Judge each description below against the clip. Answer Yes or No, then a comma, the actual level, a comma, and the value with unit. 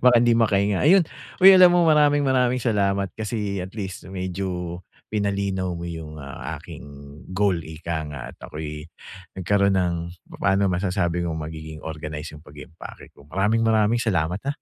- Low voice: Yes, very low, 95 Hz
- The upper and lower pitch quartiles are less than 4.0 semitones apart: No, average, 4.9 semitones